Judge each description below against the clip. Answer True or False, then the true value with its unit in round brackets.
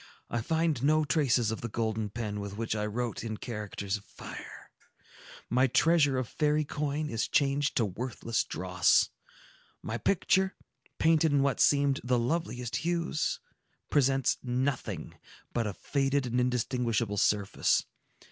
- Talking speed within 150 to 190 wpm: False (140 wpm)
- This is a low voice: True (125 Hz)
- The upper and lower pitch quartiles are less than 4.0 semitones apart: False (4.6 semitones)